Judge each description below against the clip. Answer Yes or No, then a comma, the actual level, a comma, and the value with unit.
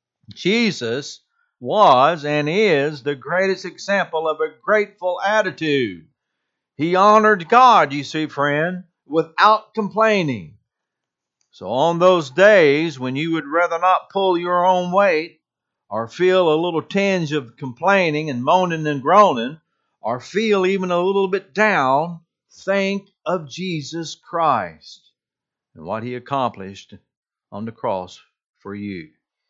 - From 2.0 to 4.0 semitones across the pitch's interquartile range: No, average, 4.7 semitones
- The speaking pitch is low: No, medium, 175 Hz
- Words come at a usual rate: No, slow, 130 wpm